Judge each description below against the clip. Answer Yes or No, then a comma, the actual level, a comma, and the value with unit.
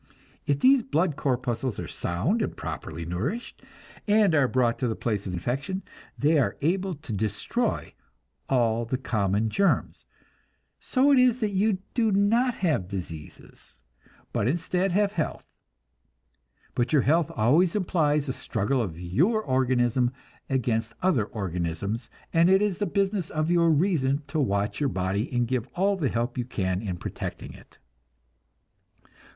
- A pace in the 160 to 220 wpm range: No, average, 150 wpm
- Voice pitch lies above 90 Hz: Yes, low, 135 Hz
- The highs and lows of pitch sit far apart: Yes, wide, 8.9 semitones